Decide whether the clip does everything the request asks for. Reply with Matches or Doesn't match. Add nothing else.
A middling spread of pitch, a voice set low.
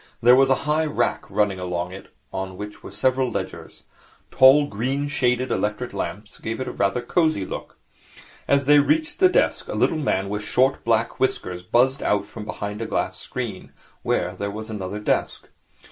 Matches